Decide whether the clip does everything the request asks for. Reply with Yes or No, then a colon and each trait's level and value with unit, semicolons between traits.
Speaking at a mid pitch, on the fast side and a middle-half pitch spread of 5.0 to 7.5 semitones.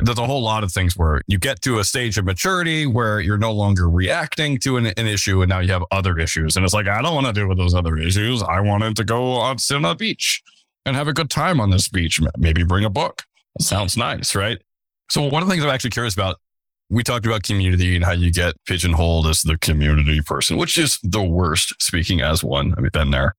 No: low, 100 Hz; fast, 250 wpm; wide, 5.5 semitones